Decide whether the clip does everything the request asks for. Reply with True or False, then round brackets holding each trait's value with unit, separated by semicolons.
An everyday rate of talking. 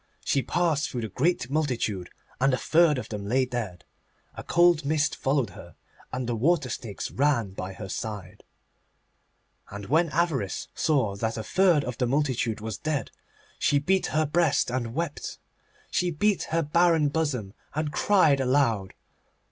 True (160 wpm)